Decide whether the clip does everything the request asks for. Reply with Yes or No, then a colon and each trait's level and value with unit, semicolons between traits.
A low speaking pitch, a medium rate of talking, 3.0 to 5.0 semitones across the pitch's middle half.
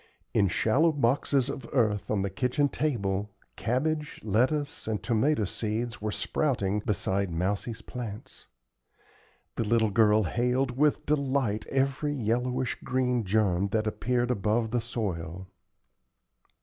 No: low, 115 Hz; slow, 125 wpm; average, 4.0 semitones